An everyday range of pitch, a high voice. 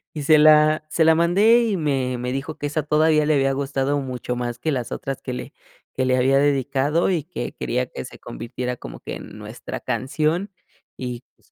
No: average, 3.4 semitones; medium, 140 Hz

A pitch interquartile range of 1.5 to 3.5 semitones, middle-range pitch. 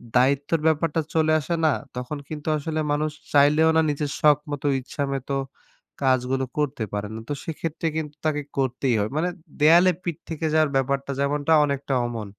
Yes: narrow, 2.6 semitones; medium, 145 Hz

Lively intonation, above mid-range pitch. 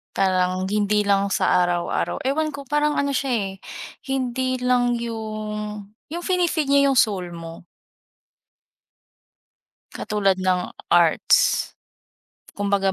Yes: wide, 5.7 semitones; high, 210 Hz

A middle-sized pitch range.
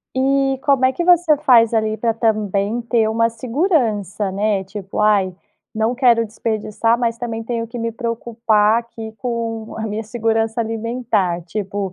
No: narrow, 1.9 semitones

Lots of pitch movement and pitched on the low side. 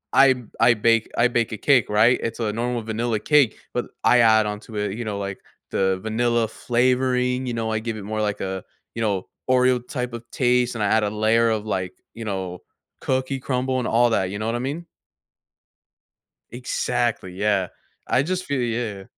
No: average, 2.7 semitones; low, 115 Hz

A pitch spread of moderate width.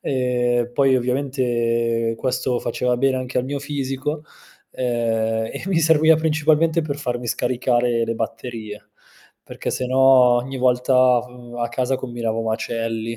No: narrow, 2.3 semitones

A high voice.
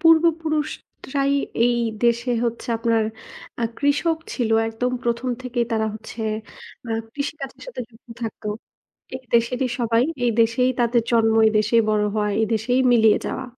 Yes: high, 235 Hz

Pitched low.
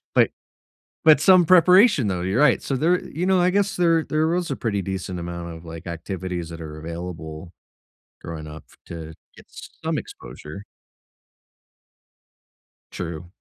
Yes: very low, 95 Hz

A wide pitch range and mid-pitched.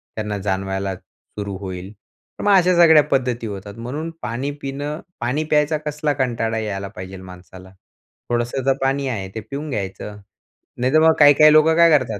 No: wide, 6.7 semitones; low, 120 Hz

